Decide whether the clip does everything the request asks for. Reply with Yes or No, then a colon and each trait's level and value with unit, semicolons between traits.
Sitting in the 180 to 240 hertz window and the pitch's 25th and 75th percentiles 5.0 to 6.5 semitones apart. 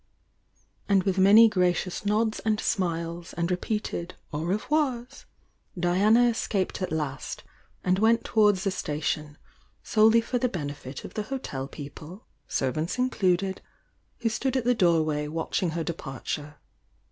Yes: medium, 185 Hz; wide, 5.4 semitones